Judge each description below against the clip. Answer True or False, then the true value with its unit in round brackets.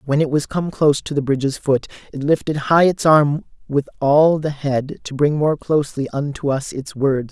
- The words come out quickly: True (215 wpm)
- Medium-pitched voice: True (145 Hz)